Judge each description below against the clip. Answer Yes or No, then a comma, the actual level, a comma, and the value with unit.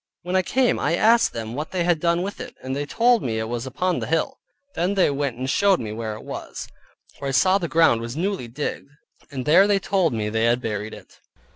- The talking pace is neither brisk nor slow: No, fast, 245 wpm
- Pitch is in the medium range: Yes, medium, 150 Hz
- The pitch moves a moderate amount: No, wide, 7.8 semitones